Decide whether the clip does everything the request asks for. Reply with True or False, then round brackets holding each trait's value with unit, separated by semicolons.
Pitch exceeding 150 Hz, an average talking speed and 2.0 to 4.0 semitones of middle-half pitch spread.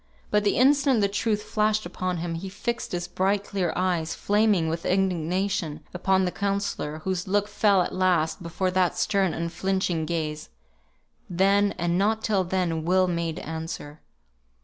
True (185 Hz; 155 wpm; 3.0 semitones)